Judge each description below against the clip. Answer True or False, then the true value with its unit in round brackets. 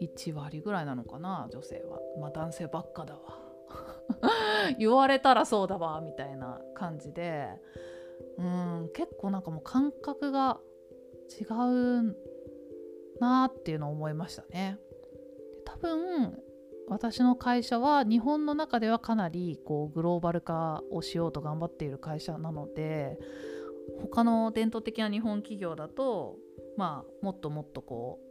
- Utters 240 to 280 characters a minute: True (270 characters per minute)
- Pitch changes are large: True (7.8 semitones)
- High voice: False (175 Hz)